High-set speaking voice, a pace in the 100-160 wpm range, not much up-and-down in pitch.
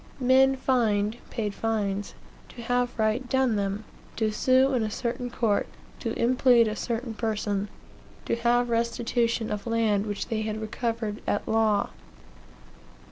Yes: high, 230 Hz; average, 140 wpm; narrow, 2.3 semitones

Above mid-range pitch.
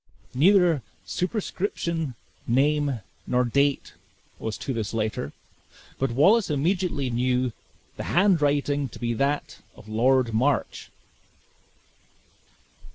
No: medium, 140 Hz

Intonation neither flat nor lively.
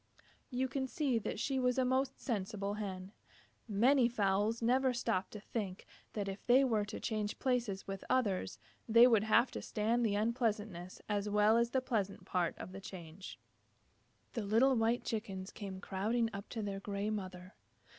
Yes: average, 3.4 semitones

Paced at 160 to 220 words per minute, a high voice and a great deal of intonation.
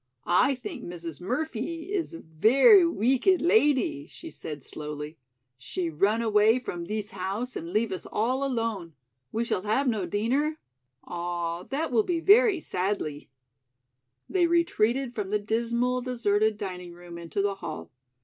No: average, 150 wpm; high, 220 Hz; wide, 7.2 semitones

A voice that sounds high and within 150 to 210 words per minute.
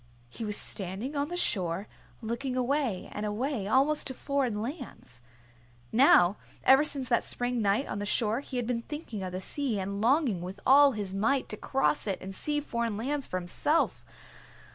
Yes: high, 235 Hz; average, 185 wpm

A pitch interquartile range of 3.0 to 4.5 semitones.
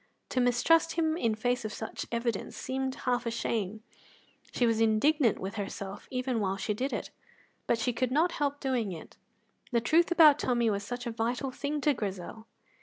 Yes: average, 3.5 semitones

